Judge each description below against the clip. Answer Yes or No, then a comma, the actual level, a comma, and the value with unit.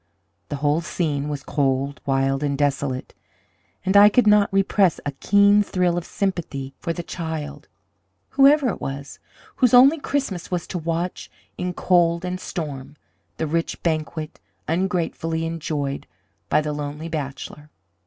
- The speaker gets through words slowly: No, average, 145 wpm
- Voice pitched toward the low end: No, medium, 165 Hz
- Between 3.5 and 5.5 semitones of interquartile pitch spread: Yes, average, 4.2 semitones